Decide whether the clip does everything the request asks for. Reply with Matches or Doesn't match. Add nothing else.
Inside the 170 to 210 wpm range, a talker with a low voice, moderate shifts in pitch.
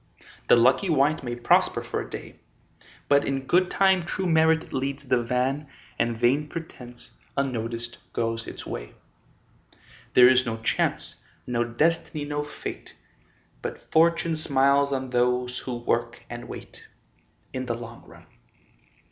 Doesn't match